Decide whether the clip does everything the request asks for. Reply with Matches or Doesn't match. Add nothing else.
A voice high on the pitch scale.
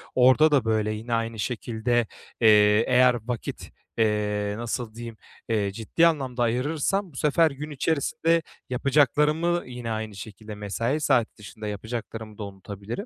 Doesn't match